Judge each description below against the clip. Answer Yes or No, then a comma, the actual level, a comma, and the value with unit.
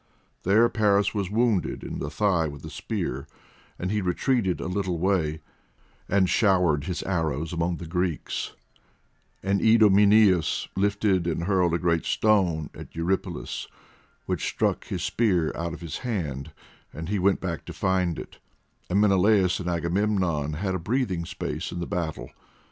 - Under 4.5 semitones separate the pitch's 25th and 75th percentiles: Yes, average, 3.3 semitones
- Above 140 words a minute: Yes, average, 155 wpm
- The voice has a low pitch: Yes, very low, 90 Hz